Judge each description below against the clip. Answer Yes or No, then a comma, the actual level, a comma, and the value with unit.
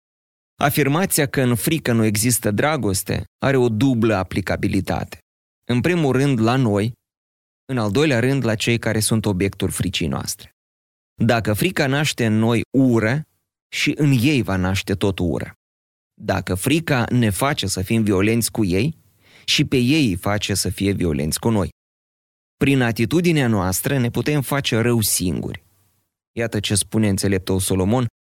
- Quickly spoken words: No, average, 155 wpm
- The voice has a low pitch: Yes, low, 110 Hz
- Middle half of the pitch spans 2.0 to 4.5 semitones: No, average, 5.3 semitones